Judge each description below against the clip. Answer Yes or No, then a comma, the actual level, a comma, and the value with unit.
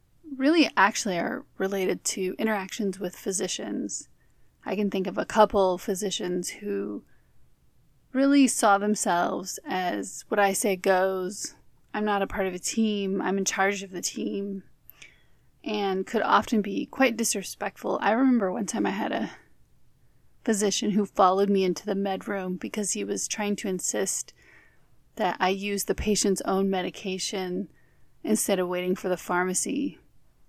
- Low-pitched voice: No, high, 200 Hz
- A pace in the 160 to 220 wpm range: No, average, 150 wpm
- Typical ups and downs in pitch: No, narrow, 2.1 semitones